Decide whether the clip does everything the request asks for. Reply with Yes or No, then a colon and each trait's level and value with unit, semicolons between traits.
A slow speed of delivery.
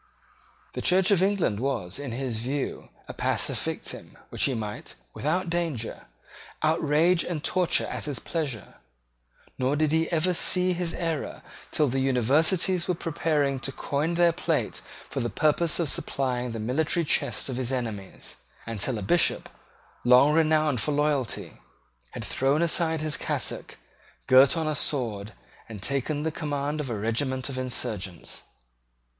No: average, 155 wpm